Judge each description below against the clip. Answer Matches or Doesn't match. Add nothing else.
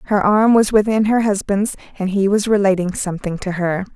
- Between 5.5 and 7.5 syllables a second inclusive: Doesn't match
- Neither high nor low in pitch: Doesn't match